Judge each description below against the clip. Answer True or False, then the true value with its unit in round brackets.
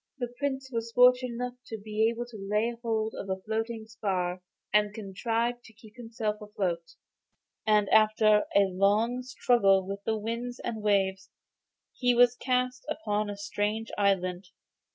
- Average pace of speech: True (155 wpm)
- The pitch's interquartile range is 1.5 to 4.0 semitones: True (3.0 semitones)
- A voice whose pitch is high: True (220 Hz)